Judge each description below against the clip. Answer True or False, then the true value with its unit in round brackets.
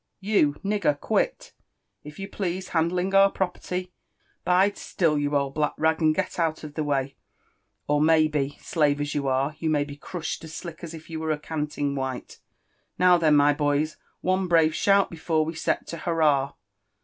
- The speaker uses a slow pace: False (195 wpm)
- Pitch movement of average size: True (3.1 semitones)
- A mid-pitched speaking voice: True (155 Hz)